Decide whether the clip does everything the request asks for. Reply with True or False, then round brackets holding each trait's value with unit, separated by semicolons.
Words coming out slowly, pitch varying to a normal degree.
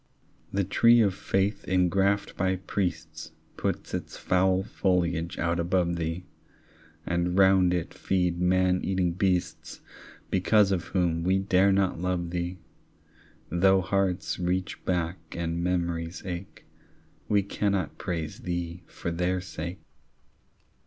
False (125 wpm; 1.8 semitones)